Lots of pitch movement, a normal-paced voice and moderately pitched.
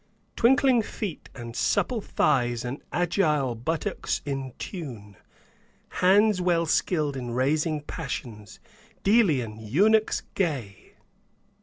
No: wide, 7.3 semitones; slow, 100 wpm; medium, 150 Hz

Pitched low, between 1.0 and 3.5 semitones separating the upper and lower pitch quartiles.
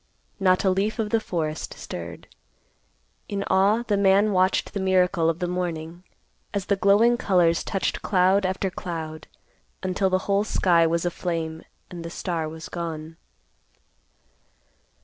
No: medium, 185 Hz; average, 3.0 semitones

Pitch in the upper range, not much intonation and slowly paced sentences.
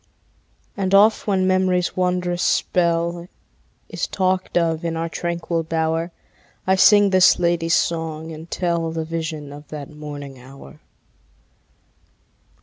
No: medium, 170 Hz; narrow, 2.2 semitones; slow, 125 wpm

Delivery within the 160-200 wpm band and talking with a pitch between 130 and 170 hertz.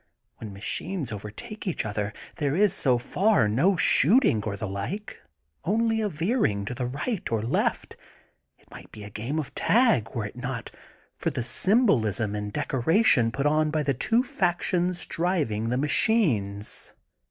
Yes: average, 165 wpm; low, 135 Hz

